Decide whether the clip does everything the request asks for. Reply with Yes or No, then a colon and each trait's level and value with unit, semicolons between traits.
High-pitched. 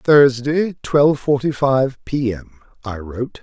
No: low, 130 Hz